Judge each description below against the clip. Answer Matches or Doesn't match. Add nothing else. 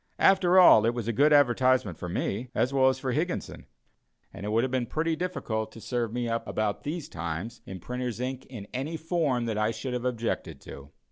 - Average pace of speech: Doesn't match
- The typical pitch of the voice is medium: Doesn't match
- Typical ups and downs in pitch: Matches